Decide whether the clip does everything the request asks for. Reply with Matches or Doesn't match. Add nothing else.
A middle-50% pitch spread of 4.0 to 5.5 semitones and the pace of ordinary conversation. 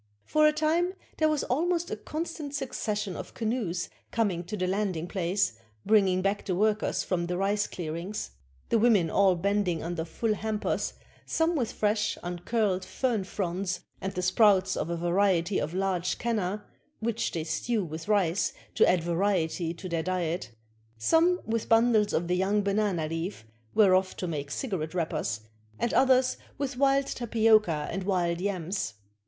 Matches